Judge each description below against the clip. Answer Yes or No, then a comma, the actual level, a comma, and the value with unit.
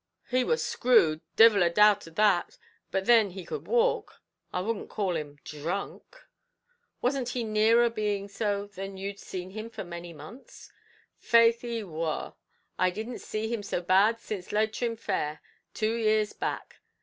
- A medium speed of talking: Yes, average, 160 wpm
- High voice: Yes, high, 210 Hz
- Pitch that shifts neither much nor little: Yes, average, 3.9 semitones